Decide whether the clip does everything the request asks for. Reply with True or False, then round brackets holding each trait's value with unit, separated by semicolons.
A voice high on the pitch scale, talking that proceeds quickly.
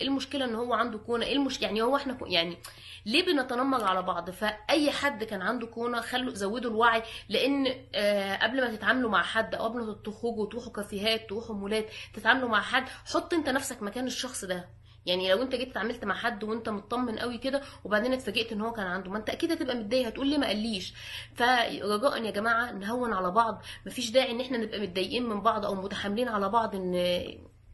True (225 Hz; 205 wpm)